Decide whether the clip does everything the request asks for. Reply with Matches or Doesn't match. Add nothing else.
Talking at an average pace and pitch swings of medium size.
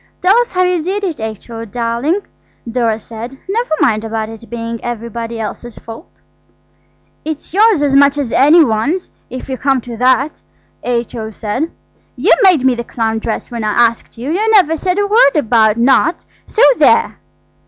Doesn't match